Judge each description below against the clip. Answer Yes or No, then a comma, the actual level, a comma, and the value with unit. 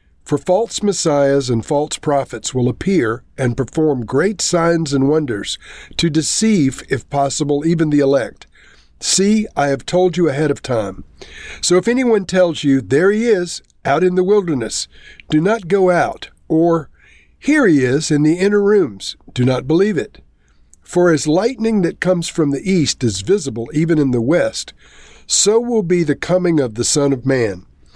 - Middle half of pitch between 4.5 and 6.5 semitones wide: Yes, average, 5.1 semitones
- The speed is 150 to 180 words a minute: Yes, average, 175 wpm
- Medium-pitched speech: Yes, medium, 155 Hz